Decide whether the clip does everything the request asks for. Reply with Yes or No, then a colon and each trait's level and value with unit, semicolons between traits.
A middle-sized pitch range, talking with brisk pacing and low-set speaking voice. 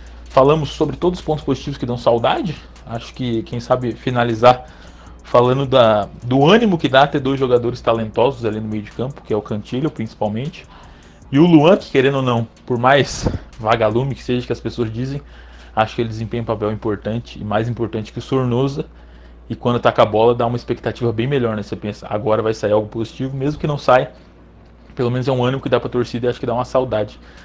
Yes: average, 3.5 semitones; fast, 220 wpm; low, 120 Hz